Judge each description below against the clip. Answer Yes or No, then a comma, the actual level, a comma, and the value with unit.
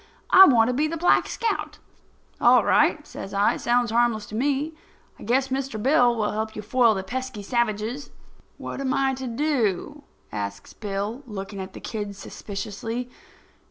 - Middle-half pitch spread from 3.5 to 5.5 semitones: Yes, average, 4.2 semitones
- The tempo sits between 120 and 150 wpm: No, average, 170 wpm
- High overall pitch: Yes, high, 235 Hz